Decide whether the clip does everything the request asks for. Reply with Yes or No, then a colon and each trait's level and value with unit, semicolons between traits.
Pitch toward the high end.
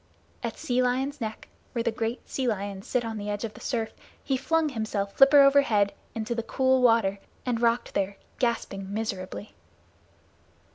Yes: high, 230 Hz